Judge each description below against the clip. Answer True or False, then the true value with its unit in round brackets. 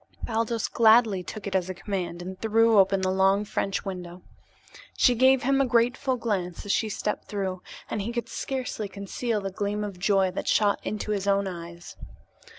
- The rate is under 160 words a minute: False (185 wpm)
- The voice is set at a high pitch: True (200 Hz)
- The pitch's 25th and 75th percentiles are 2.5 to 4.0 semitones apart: True (3.1 semitones)